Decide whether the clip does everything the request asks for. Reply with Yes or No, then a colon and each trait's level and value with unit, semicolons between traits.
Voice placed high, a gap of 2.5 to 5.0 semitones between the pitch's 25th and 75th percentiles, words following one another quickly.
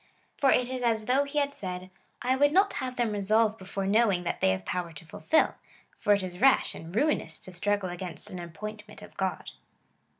No: high, 210 Hz; wide, 5.6 semitones; fast, 220 wpm